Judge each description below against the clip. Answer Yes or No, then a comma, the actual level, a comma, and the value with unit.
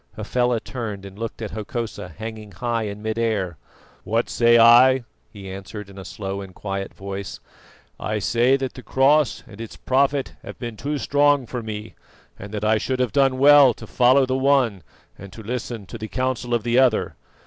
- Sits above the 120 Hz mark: No, low, 115 Hz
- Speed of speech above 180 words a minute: Yes, average, 190 wpm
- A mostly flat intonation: No, average, 3.7 semitones